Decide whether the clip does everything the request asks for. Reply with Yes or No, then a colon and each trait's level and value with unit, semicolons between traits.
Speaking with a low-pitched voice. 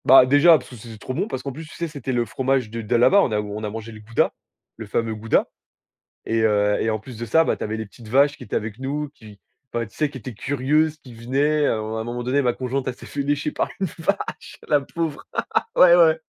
Yes: low, 125 Hz